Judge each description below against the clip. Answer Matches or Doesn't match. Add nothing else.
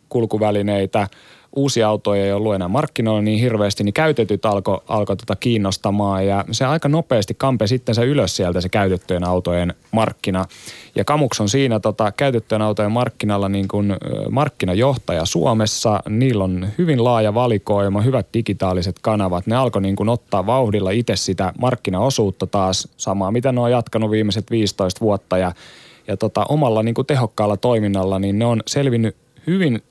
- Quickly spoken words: Matches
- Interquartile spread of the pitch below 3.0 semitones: Doesn't match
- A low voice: Matches